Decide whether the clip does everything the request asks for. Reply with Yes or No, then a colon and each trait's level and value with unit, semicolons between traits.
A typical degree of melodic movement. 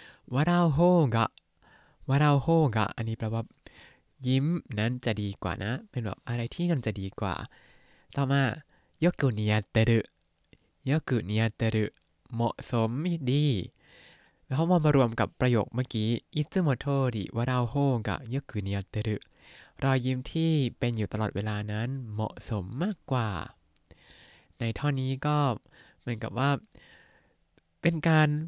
Yes: average, 4.6 semitones